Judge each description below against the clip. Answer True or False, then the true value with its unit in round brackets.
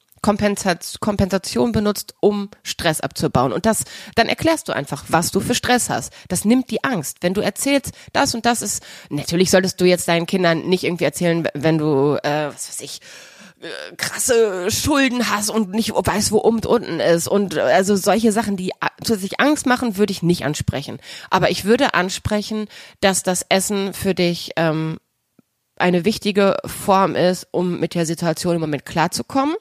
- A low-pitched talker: False (195 Hz)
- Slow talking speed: False (180 wpm)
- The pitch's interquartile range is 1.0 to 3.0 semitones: False (4.4 semitones)